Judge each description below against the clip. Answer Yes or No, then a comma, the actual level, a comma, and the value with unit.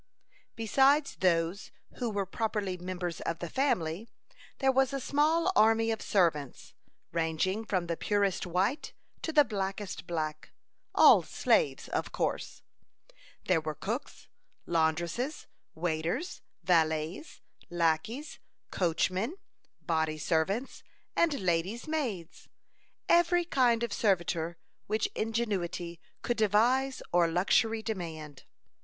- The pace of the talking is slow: Yes, slow, 110 wpm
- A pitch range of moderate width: No, wide, 6.0 semitones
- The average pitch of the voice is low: No, high, 195 Hz